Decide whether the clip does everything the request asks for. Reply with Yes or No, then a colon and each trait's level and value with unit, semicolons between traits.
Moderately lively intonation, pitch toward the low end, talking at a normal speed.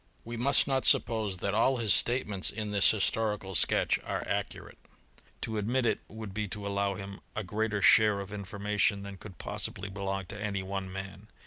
No: narrow, 1.9 semitones; low, 105 Hz; average, 185 wpm